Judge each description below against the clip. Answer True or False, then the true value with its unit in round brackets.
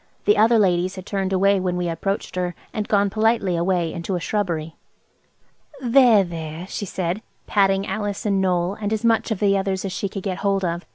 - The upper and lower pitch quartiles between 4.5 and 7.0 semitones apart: False (2.5 semitones)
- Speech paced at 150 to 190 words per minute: False (205 wpm)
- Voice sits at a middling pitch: False (195 Hz)